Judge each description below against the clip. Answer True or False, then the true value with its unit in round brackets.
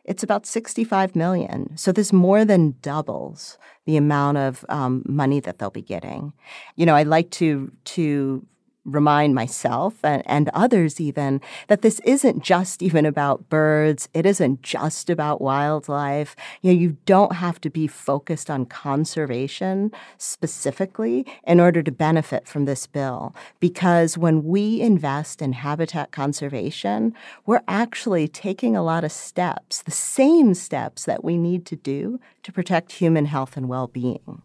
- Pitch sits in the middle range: True (160 Hz)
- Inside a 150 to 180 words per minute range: True (155 wpm)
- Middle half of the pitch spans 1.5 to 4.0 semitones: False (4.6 semitones)